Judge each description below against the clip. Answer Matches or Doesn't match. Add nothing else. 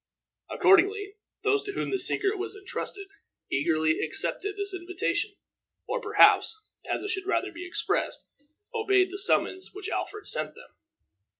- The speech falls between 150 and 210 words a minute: Doesn't match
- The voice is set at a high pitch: Matches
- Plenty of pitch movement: Doesn't match